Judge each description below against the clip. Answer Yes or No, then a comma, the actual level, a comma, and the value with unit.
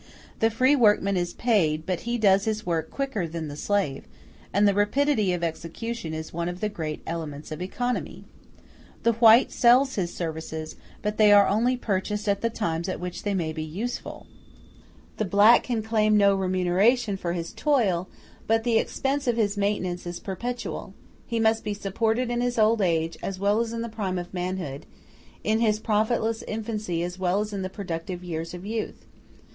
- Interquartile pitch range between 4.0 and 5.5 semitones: Yes, average, 4.3 semitones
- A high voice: Yes, high, 205 Hz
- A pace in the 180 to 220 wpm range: Yes, average, 185 wpm